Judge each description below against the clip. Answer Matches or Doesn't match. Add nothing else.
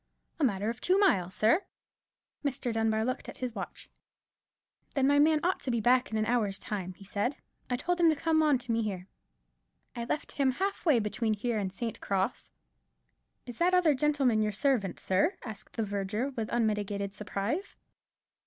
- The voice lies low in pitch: Doesn't match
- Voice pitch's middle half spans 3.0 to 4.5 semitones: Doesn't match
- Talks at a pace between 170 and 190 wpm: Matches